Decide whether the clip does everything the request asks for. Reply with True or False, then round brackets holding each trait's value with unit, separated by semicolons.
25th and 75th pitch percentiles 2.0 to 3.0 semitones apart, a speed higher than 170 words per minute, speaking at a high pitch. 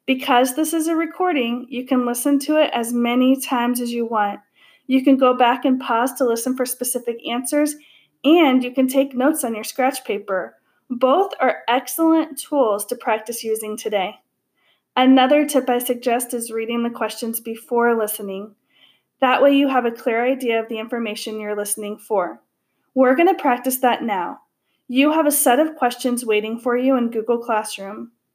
True (2.7 semitones; 180 wpm; 245 Hz)